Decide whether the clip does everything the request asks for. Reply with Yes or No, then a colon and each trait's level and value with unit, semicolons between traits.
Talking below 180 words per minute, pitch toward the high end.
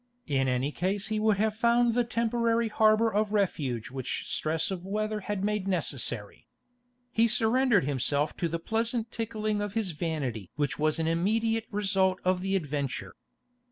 Yes: average, 160 wpm; high, 200 Hz